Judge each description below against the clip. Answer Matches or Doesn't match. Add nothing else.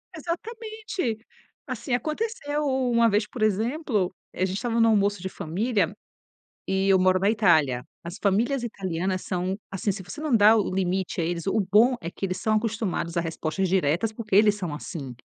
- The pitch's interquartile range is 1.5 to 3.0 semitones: Doesn't match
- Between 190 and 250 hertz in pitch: Matches